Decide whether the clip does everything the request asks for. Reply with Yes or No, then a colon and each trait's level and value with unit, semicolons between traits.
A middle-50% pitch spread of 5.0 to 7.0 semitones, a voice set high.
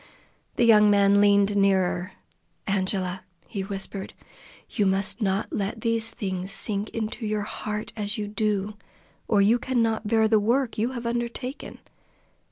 No: narrow, 2.4 semitones; high, 210 Hz